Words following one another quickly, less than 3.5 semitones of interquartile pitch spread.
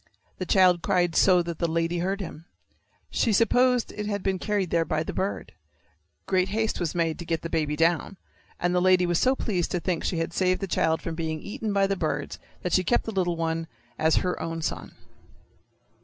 Yes: fast, 215 wpm; average, 2.9 semitones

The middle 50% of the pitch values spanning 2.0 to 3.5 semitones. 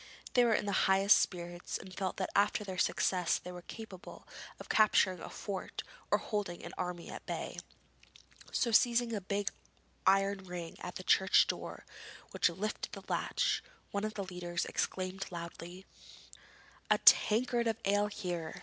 Yes: narrow, 2.6 semitones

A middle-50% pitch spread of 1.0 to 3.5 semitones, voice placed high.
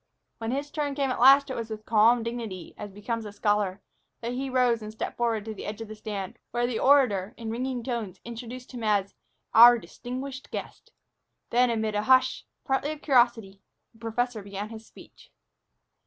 Yes: average, 2.9 semitones; high, 230 Hz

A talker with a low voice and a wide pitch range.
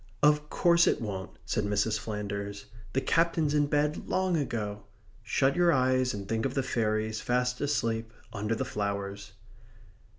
Yes: low, 115 Hz; wide, 5.7 semitones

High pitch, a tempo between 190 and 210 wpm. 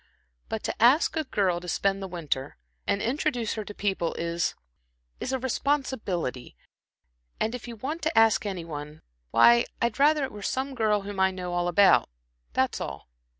No: high, 205 Hz; average, 180 wpm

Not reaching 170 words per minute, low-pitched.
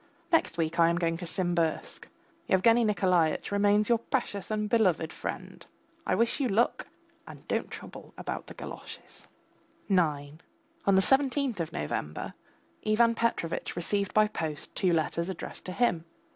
No: average, 150 wpm; high, 190 Hz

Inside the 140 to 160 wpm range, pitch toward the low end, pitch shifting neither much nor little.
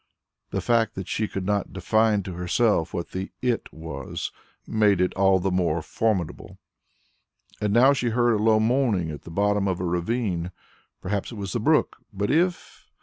No: average, 180 wpm; low, 100 Hz; average, 3.9 semitones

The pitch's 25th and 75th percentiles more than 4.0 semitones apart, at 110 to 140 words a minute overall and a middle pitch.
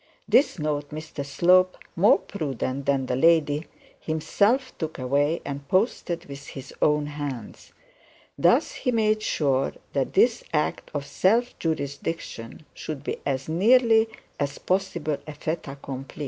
Yes: average, 4.7 semitones; slow, 135 wpm; medium, 150 Hz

